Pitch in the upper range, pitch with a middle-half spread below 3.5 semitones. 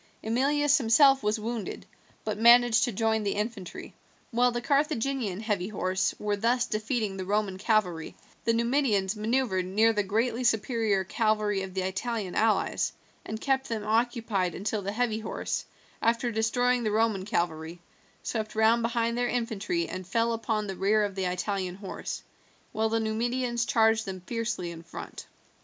Yes: high, 220 Hz; average, 3.0 semitones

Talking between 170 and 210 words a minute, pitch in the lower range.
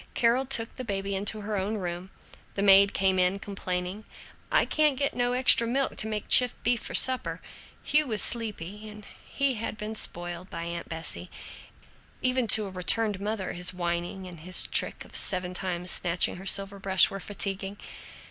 No: average, 180 wpm; high, 200 Hz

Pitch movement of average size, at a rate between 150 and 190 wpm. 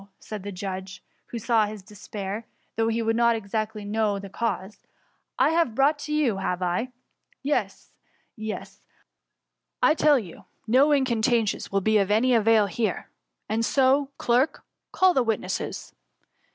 Yes: average, 3.7 semitones; average, 165 wpm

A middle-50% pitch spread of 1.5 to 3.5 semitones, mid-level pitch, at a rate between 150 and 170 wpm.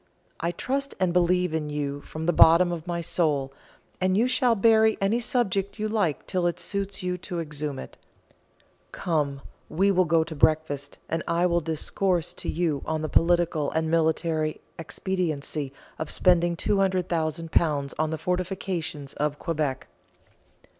Yes: average, 2.9 semitones; medium, 170 Hz; average, 155 wpm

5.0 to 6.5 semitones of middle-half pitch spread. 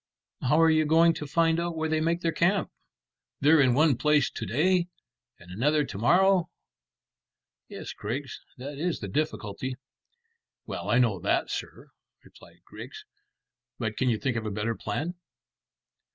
Yes: wide, 5.4 semitones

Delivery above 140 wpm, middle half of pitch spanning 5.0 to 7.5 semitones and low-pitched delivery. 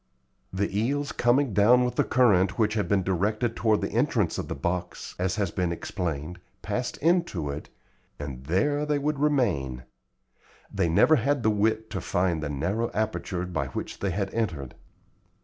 Yes: average, 170 wpm; wide, 5.4 semitones; low, 100 Hz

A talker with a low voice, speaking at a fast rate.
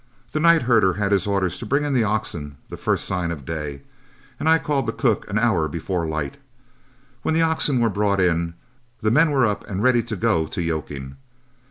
Yes: low, 100 Hz; fast, 210 wpm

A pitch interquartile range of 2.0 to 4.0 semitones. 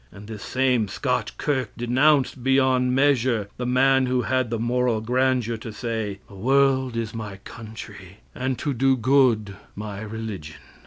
Yes: average, 3.1 semitones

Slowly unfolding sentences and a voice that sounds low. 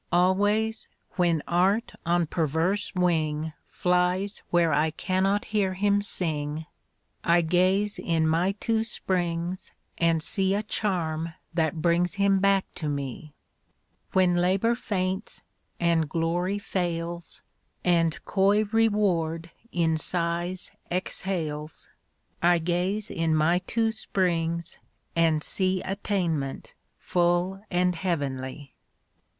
No: slow, 110 wpm; medium, 175 Hz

